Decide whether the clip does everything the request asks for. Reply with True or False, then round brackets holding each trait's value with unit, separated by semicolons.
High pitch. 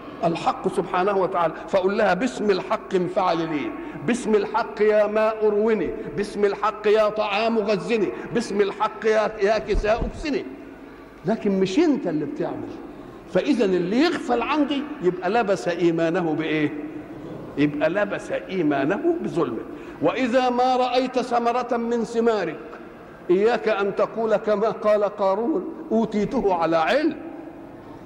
True (215 Hz)